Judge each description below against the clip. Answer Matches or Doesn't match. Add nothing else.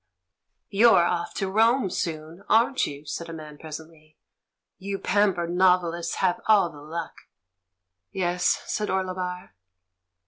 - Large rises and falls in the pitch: Doesn't match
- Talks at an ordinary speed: Doesn't match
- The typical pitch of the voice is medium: Matches